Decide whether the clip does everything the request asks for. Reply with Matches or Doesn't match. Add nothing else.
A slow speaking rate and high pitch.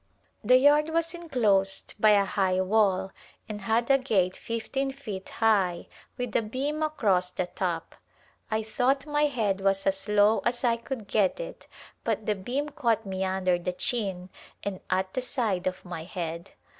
Doesn't match